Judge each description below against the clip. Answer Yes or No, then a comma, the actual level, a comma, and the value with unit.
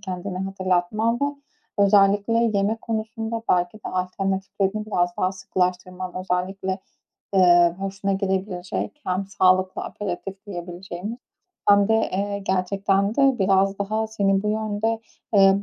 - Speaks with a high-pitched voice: Yes, high, 195 Hz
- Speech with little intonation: Yes, narrow, 1.8 semitones